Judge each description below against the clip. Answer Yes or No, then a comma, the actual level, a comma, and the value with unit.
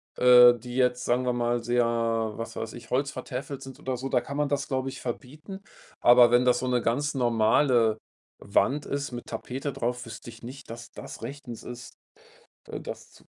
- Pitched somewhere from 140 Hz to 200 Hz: No, low, 125 Hz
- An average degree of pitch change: No, narrow, 2.1 semitones